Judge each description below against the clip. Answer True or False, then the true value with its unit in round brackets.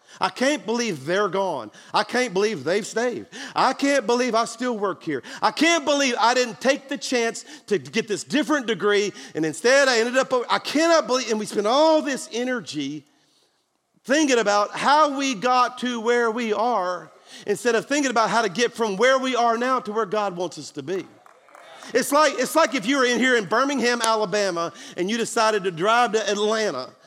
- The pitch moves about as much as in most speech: True (3.8 semitones)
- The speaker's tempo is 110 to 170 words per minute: False (200 wpm)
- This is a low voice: False (235 Hz)